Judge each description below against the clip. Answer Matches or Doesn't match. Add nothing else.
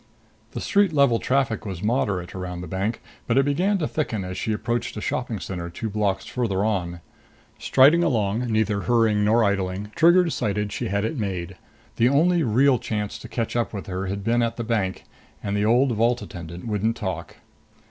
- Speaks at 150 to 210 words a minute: Matches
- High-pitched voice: Doesn't match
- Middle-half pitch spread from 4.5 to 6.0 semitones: Doesn't match